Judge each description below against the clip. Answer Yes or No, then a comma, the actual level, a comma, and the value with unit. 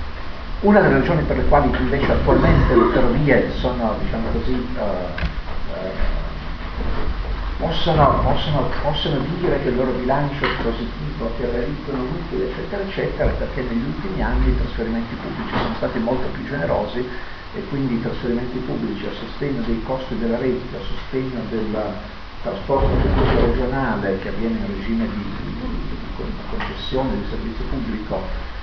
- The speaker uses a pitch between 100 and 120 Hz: Yes, low, 115 Hz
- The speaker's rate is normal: Yes, average, 140 wpm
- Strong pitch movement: Yes, wide, 5.8 semitones